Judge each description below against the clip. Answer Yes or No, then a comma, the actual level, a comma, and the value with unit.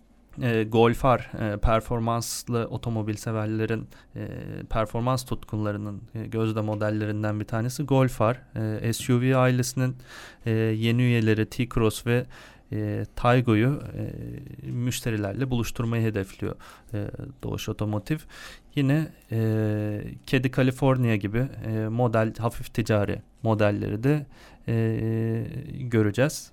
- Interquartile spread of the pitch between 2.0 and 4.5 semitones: Yes, average, 2.9 semitones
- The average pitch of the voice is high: No, low, 115 Hz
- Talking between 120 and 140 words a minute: No, average, 100 wpm